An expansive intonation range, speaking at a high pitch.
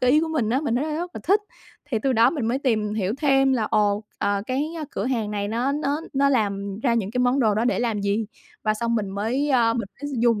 No: average, 4.3 semitones; high, 235 Hz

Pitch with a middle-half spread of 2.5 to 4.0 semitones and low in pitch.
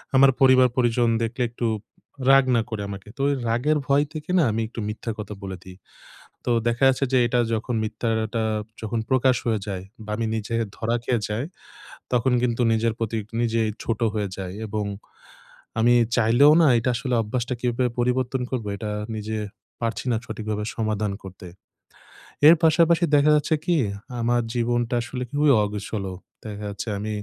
Yes: average, 2.9 semitones; low, 115 Hz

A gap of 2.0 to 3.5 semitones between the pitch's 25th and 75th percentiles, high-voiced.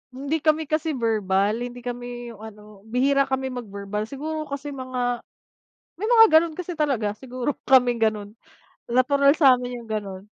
No: average, 4.2 semitones; very high, 250 Hz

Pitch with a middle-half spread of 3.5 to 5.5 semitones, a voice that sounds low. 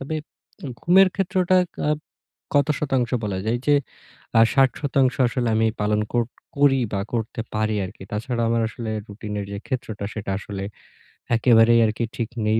Yes: average, 4.0 semitones; low, 115 Hz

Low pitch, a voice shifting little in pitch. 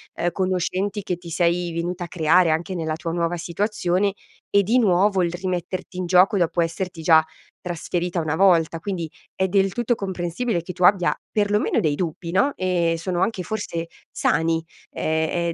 No: medium, 180 Hz; narrow, 2.2 semitones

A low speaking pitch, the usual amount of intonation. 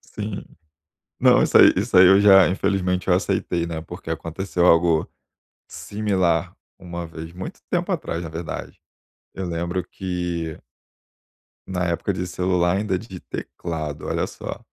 No: very low, 90 Hz; narrow, 2.1 semitones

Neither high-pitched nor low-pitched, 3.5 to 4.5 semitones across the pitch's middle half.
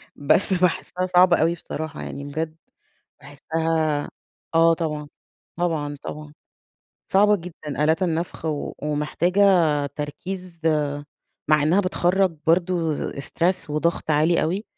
No: medium, 165 Hz; average, 2.9 semitones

